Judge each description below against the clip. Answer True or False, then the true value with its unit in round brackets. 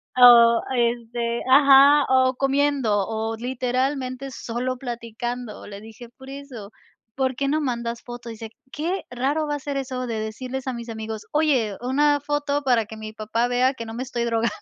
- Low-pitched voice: False (245 Hz)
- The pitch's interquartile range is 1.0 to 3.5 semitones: True (2.8 semitones)